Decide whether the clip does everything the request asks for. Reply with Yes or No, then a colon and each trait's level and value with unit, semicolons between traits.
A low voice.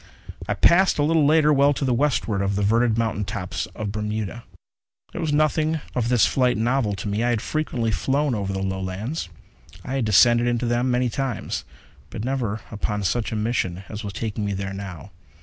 Yes: low, 115 Hz